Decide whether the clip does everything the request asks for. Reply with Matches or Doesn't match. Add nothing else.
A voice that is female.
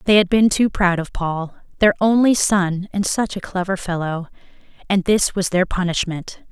Matches